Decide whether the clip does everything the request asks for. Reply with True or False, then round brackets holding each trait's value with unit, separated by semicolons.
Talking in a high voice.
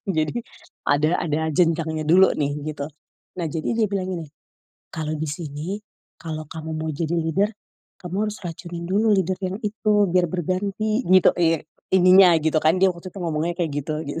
False (170 Hz)